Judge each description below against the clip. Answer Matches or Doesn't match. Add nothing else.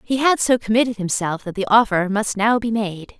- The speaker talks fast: Matches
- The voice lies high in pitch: Matches